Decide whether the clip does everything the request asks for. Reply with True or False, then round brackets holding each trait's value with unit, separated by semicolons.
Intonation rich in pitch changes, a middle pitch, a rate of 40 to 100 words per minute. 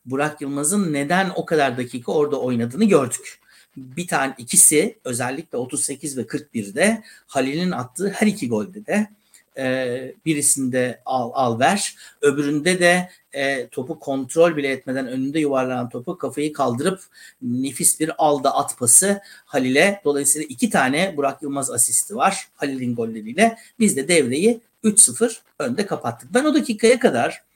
False (6.8 semitones; 150 Hz; 140 wpm)